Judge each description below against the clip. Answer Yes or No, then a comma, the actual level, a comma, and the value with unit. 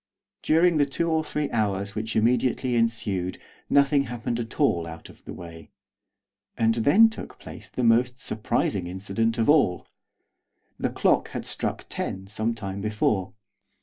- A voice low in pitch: Yes, low, 115 Hz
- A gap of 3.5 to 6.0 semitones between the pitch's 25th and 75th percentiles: Yes, average, 5.1 semitones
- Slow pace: No, average, 150 wpm